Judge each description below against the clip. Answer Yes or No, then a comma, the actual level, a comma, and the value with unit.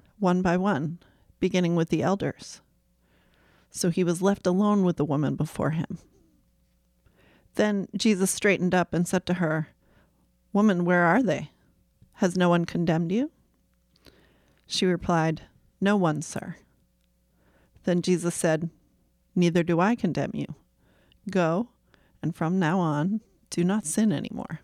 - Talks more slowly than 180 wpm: Yes, average, 140 wpm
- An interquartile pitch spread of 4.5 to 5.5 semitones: No, average, 3.3 semitones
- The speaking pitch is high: No, medium, 175 Hz